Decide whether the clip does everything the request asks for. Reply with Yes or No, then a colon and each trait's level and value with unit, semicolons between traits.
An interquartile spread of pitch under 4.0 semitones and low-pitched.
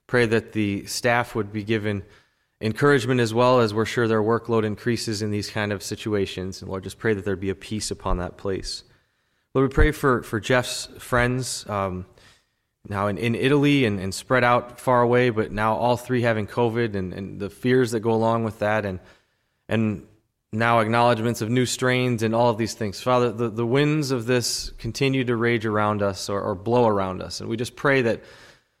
Yes: average, 2.9 semitones; low, 115 Hz